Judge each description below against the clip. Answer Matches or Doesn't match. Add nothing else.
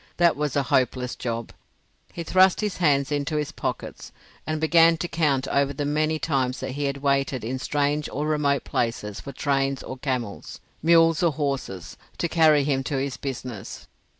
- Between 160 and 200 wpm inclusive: Matches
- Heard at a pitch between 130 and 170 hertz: Matches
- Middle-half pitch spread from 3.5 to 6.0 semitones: Doesn't match